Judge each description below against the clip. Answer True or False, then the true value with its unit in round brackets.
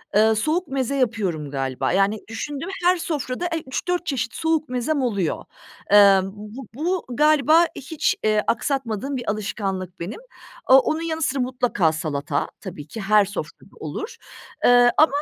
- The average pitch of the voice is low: False (245 Hz)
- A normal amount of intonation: False (7.0 semitones)